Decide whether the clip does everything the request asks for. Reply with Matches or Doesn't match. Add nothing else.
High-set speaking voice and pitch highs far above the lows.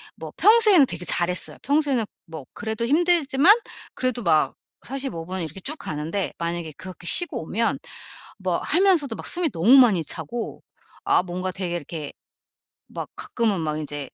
Matches